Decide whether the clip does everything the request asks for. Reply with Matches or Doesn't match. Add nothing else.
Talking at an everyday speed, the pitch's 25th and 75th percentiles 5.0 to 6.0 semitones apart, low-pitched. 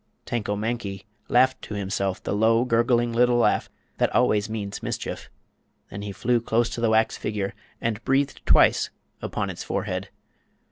Doesn't match